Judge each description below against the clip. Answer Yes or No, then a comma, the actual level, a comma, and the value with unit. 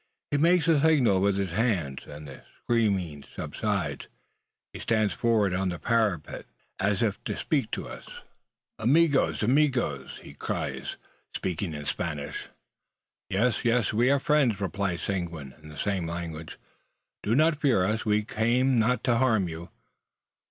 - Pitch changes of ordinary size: No, wide, 6.1 semitones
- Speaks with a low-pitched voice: Yes, low, 105 Hz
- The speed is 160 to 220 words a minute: No, average, 150 wpm